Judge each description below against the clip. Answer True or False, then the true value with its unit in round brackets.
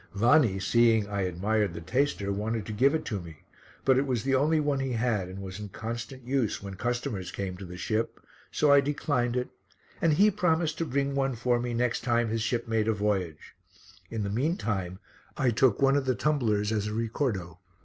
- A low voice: True (115 Hz)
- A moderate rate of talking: False (210 wpm)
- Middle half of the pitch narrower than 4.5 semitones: False (4.8 semitones)